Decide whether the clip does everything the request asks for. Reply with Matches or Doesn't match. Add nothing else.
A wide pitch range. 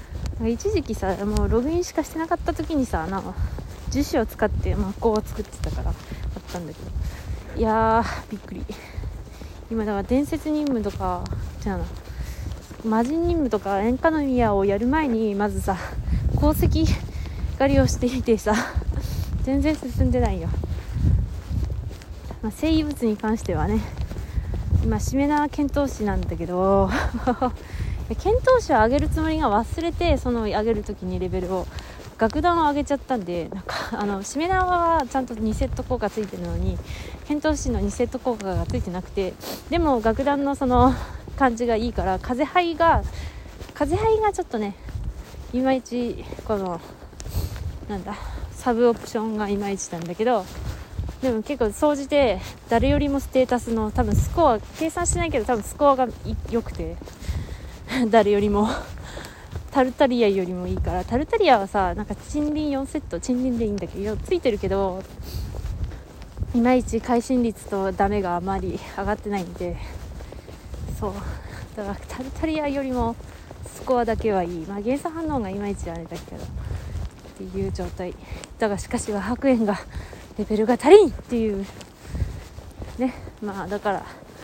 Matches